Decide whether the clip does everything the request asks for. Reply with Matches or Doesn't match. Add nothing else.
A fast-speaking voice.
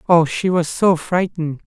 Doesn't match